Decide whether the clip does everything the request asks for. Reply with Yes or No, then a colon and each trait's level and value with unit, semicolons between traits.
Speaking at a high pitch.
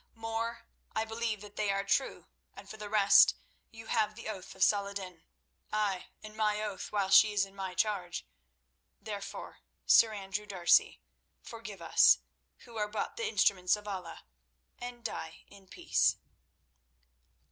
Yes: high, 210 Hz